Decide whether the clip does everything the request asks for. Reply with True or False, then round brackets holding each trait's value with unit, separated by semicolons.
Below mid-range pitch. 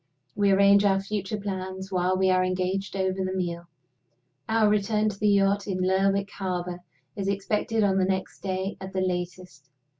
False (190 Hz)